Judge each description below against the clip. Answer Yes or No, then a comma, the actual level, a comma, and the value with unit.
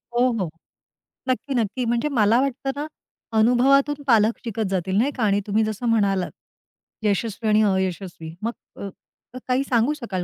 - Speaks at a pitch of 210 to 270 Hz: Yes, high, 225 Hz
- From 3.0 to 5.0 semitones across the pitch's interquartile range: Yes, average, 4.0 semitones